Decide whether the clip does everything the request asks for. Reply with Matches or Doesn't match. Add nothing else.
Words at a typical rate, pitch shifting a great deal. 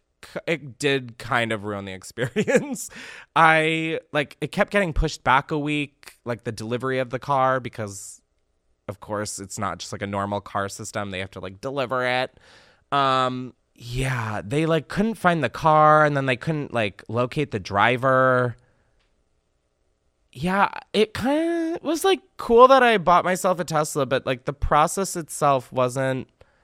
Matches